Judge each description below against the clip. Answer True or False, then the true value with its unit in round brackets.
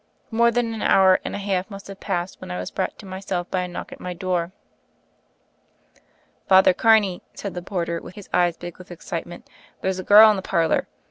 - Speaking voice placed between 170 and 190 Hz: True (185 Hz)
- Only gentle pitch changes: True (2.2 semitones)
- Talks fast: True (210 wpm)